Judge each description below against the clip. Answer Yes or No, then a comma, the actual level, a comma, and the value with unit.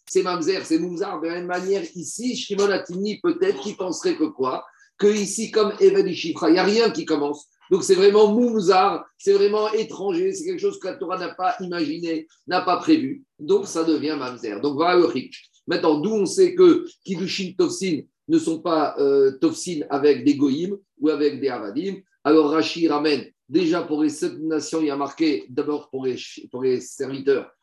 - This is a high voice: Yes, high, 195 Hz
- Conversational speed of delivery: Yes, average, 190 wpm